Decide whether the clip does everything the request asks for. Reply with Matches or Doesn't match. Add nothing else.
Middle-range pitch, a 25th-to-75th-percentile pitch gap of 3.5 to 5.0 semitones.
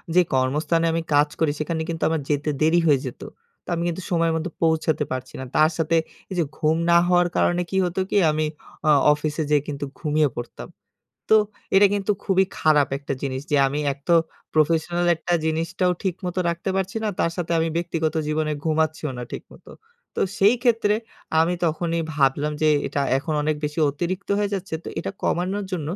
Doesn't match